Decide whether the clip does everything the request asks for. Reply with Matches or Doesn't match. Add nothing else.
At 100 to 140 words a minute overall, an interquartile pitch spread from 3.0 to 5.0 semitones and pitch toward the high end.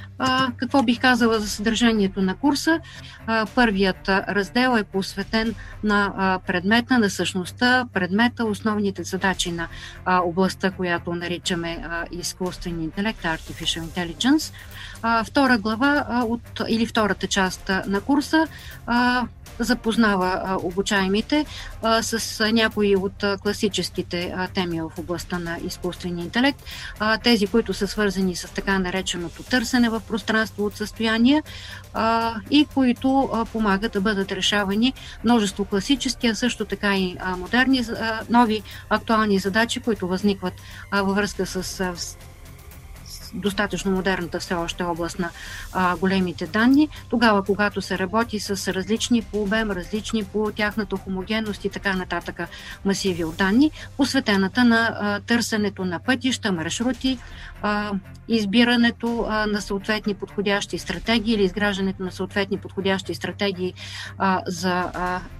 Matches